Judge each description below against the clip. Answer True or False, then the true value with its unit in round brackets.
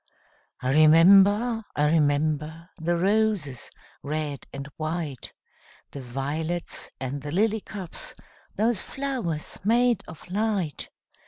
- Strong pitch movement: True (5.7 semitones)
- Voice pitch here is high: False (165 Hz)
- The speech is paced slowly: True (105 wpm)